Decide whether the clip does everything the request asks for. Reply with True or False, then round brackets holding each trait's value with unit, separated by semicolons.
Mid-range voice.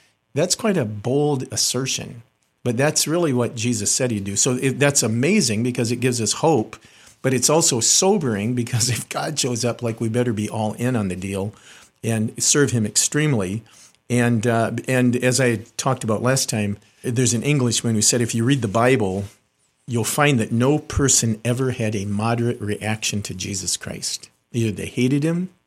False (120 Hz)